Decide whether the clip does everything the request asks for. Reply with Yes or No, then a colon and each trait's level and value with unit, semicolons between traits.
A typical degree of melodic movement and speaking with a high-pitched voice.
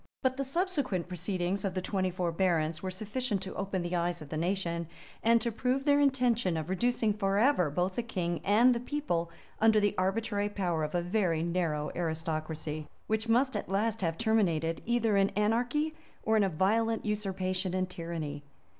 Yes: average, 4.7 semitones; high, 195 Hz